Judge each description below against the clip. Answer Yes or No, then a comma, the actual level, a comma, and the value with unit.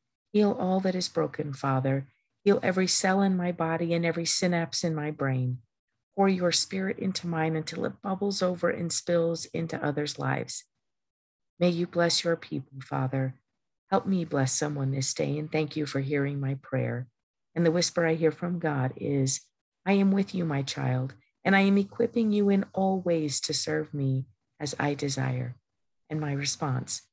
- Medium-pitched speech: Yes, medium, 160 Hz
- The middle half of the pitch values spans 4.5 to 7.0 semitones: Yes, average, 4.8 semitones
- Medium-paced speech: Yes, average, 180 wpm